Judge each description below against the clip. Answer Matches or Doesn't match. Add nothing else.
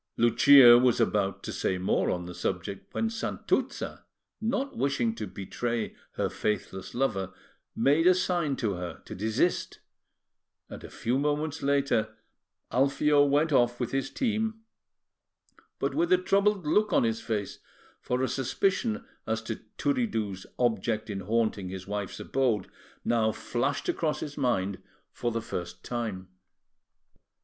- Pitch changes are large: Matches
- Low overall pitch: Matches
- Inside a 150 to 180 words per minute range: Doesn't match